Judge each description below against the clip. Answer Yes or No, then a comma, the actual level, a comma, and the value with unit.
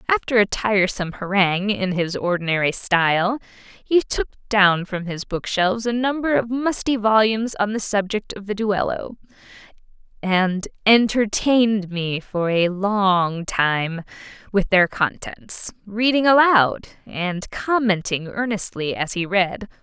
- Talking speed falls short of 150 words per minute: Yes, slow, 135 wpm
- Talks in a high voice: Yes, high, 200 Hz